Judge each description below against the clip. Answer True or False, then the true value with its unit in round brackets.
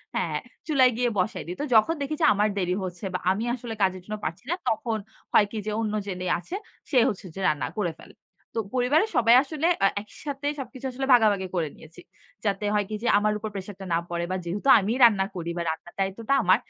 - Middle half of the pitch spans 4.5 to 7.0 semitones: True (4.8 semitones)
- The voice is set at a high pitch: True (210 Hz)